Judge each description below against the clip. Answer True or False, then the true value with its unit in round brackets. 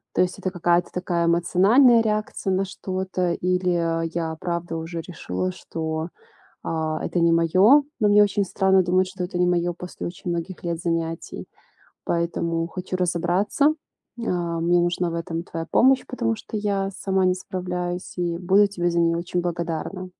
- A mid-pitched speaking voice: True (175 Hz)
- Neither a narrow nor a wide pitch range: False (1.9 semitones)